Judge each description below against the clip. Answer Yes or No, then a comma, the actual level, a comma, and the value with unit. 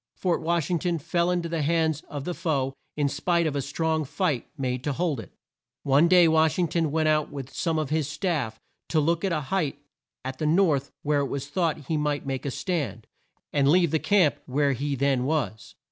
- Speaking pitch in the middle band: Yes, medium, 155 Hz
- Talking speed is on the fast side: Yes, fast, 220 wpm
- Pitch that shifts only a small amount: No, average, 3.2 semitones